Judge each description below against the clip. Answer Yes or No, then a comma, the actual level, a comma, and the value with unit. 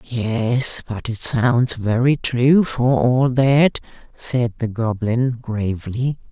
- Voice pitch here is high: No, low, 120 Hz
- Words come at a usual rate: No, slow, 125 wpm